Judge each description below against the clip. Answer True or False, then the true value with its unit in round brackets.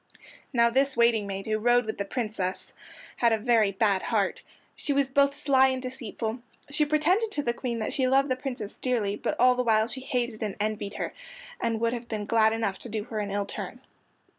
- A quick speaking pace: True (215 wpm)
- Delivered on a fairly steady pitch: False (3.3 semitones)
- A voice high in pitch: True (235 Hz)